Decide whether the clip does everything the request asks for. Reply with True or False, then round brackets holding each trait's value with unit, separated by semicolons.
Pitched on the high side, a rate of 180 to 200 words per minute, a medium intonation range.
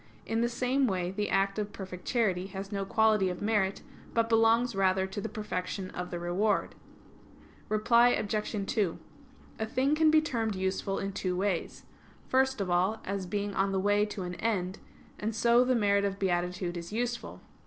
True (200 Hz; 185 wpm; 3.0 semitones)